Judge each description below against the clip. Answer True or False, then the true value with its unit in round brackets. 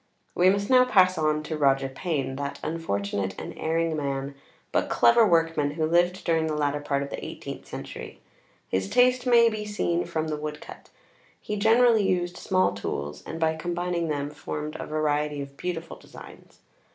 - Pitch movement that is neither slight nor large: True (4.1 semitones)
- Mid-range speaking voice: True (160 Hz)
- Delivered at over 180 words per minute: False (175 wpm)